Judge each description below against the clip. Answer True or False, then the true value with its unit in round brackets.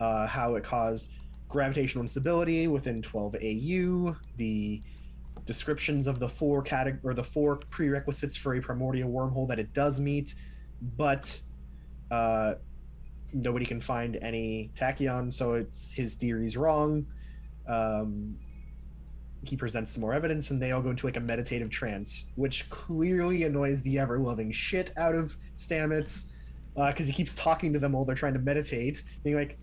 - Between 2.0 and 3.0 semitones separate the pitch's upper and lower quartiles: False (4.7 semitones)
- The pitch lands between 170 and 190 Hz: False (125 Hz)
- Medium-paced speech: True (155 wpm)